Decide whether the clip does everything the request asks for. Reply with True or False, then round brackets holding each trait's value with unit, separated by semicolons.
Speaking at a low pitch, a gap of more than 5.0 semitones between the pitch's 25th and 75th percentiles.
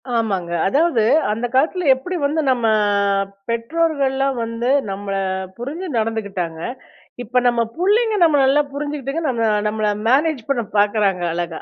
False (245 Hz; 5.6 semitones)